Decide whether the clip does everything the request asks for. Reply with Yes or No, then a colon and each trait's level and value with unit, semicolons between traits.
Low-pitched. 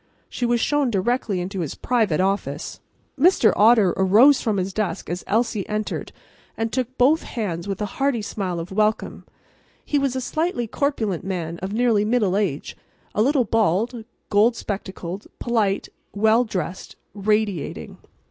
No: high, 215 Hz